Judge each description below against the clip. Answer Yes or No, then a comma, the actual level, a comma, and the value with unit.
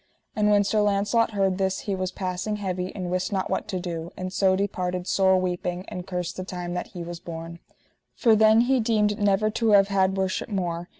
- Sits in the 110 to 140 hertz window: No, high, 190 Hz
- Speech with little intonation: Yes, narrow, 2.3 semitones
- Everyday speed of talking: No, fast, 215 wpm